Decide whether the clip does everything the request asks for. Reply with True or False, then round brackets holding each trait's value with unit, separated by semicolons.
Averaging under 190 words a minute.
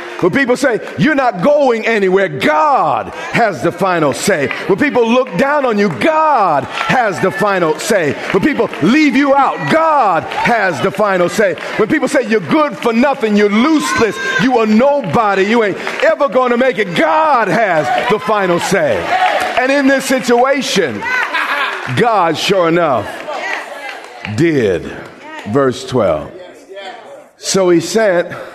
True (145 wpm)